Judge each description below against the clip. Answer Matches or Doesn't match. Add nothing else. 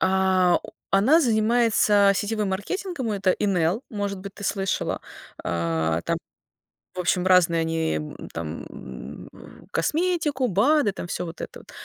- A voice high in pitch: Matches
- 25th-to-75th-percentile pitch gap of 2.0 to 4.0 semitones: Doesn't match